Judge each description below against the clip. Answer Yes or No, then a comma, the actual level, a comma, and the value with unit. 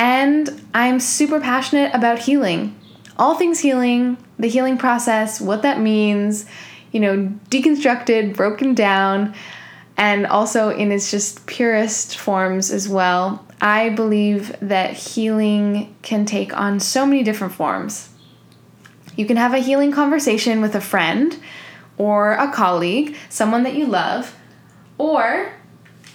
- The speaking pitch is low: No, high, 215 Hz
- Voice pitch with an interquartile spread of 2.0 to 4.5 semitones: Yes, average, 4.1 semitones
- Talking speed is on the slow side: Yes, slow, 130 wpm